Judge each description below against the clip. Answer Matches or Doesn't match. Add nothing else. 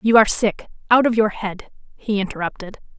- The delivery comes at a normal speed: Matches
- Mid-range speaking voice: Doesn't match